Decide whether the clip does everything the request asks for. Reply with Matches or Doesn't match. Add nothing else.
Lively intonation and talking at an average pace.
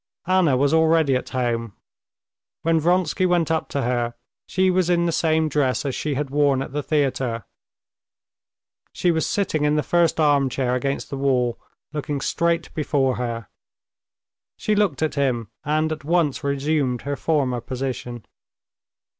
Doesn't match